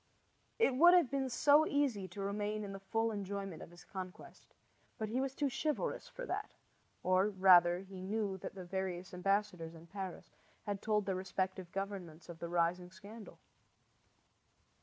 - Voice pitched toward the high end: Yes, high, 195 Hz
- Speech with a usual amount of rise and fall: Yes, average, 3.1 semitones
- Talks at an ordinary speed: Yes, average, 165 wpm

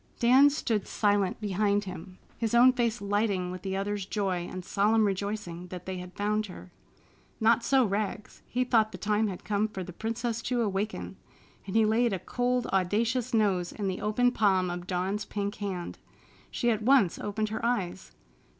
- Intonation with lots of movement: No, average, 3.1 semitones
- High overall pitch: Yes, high, 205 Hz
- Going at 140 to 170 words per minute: No, average, 180 wpm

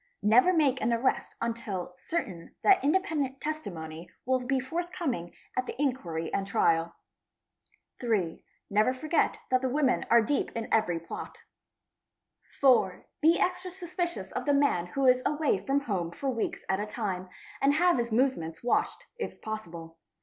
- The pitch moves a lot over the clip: Yes, wide, 7.0 semitones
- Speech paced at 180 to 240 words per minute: No, average, 155 wpm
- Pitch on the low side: No, very high, 250 Hz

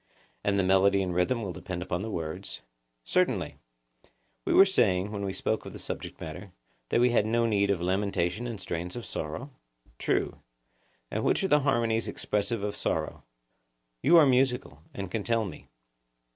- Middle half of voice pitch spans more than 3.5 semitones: Yes, average, 4.3 semitones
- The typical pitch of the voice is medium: No, low, 100 Hz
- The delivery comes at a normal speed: Yes, average, 175 wpm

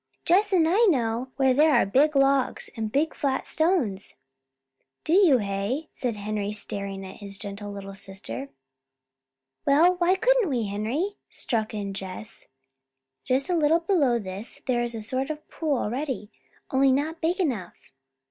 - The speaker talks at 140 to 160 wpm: Yes, average, 155 wpm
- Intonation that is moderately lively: No, wide, 7.3 semitones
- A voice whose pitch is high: Yes, very high, 255 Hz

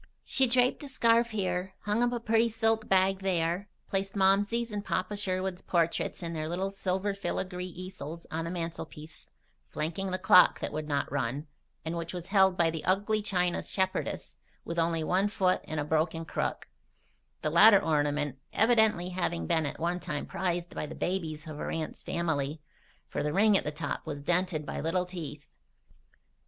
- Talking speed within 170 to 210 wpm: Yes, average, 180 wpm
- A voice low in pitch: No, medium, 180 Hz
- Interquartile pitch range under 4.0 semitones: Yes, average, 3.4 semitones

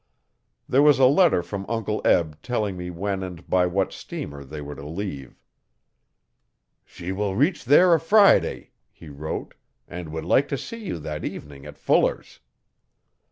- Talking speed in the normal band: Yes, average, 160 wpm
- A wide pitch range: Yes, wide, 8.6 semitones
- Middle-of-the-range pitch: No, very low, 95 Hz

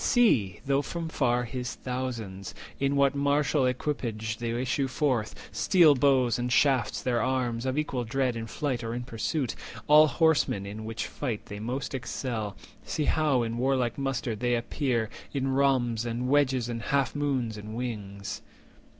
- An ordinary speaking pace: Yes, average, 160 wpm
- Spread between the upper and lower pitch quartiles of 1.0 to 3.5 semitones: Yes, average, 3.1 semitones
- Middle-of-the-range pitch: No, low, 125 Hz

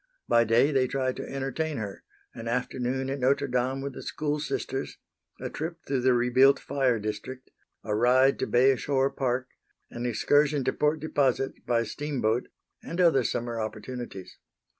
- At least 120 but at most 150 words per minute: No, average, 160 wpm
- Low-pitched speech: Yes, low, 130 Hz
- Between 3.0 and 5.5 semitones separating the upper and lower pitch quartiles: No, narrow, 2.4 semitones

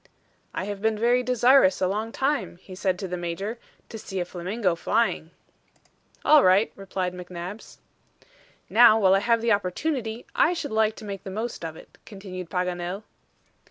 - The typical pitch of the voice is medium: No, high, 200 Hz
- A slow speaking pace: No, average, 170 wpm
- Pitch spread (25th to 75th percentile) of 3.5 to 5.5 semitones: Yes, average, 3.9 semitones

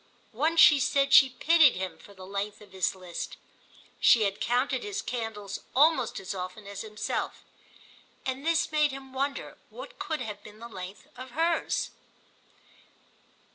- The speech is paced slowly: No, average, 145 wpm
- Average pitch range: No, wide, 6.2 semitones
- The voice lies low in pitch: No, high, 245 Hz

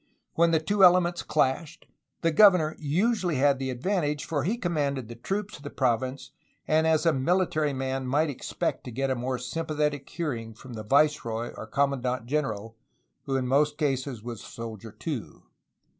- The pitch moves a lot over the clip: No, average, 4.0 semitones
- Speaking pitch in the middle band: Yes, medium, 145 Hz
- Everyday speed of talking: Yes, average, 175 wpm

